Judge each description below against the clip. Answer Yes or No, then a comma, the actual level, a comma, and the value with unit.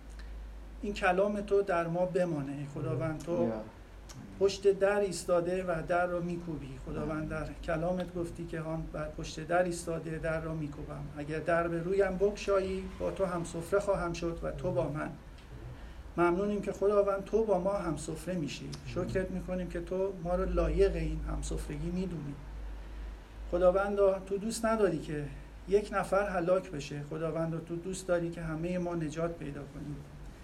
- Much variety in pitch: No, average, 3.5 semitones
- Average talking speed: No, fast, 165 wpm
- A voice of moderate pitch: Yes, medium, 170 Hz